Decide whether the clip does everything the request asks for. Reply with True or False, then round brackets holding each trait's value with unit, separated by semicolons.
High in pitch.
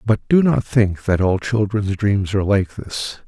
False (100 Hz)